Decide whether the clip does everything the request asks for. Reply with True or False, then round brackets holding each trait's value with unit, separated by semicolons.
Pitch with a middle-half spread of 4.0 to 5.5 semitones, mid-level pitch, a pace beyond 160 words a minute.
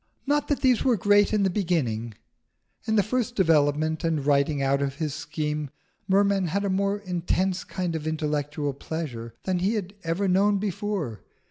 True (5.2 semitones; 175 Hz; 170 wpm)